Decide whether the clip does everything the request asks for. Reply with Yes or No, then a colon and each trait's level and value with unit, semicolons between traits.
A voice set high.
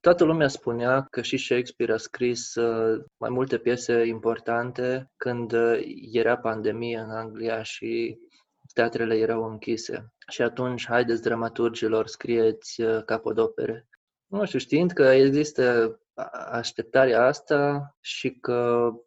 No: low, 120 Hz